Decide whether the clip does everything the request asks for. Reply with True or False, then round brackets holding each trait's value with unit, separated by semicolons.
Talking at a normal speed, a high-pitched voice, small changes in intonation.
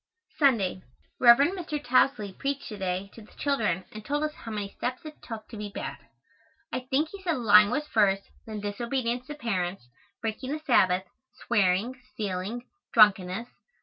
False (165 wpm; 225 Hz; 4.9 semitones)